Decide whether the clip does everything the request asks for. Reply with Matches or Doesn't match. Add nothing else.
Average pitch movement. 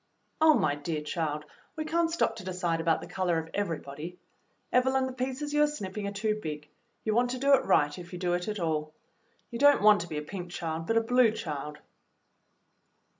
Doesn't match